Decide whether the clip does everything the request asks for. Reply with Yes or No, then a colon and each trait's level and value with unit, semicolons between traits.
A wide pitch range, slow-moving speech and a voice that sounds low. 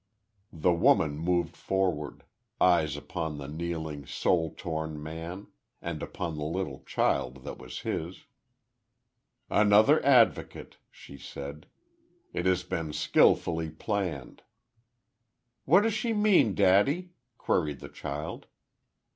No: average, 4.1 semitones; slow, 115 wpm; very low, 85 Hz